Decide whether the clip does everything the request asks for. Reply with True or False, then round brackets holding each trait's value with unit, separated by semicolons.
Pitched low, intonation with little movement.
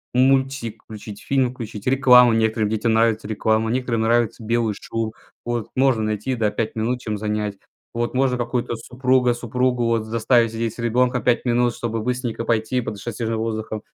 True (115 Hz; 2.1 semitones)